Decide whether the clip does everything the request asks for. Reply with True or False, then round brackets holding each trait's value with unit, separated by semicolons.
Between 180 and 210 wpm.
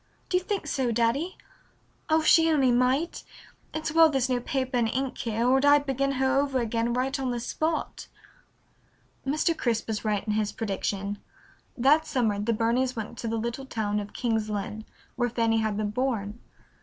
True (185 wpm)